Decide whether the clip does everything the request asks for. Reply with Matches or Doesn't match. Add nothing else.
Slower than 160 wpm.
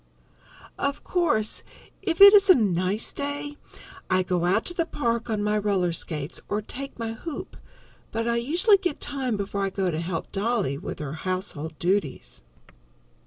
Doesn't match